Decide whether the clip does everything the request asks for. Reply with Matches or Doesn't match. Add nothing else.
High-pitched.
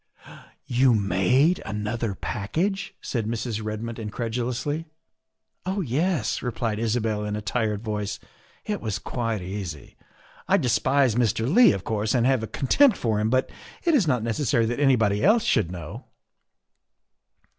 Doesn't match